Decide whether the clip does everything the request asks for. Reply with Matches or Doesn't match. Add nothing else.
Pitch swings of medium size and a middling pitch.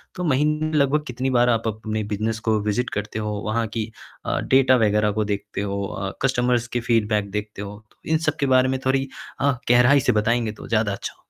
Doesn't match